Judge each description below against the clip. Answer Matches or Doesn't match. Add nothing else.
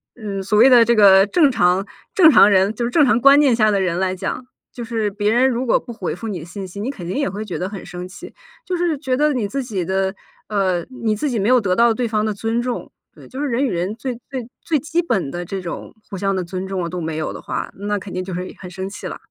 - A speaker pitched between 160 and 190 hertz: Doesn't match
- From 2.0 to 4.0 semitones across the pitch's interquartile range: Doesn't match